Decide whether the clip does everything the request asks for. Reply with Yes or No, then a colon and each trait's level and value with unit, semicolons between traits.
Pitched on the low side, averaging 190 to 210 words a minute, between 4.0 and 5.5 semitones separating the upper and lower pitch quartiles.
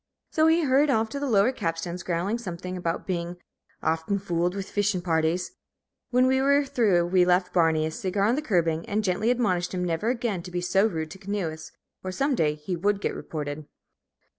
No: medium, 185 Hz; average, 200 wpm; average, 4.6 semitones